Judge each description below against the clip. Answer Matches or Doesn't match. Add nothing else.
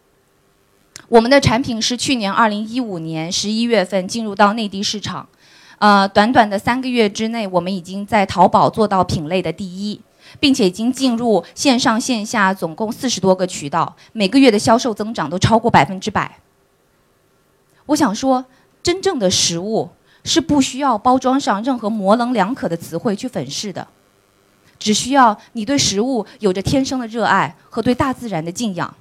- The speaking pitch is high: Matches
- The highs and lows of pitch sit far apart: Doesn't match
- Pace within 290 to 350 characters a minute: Doesn't match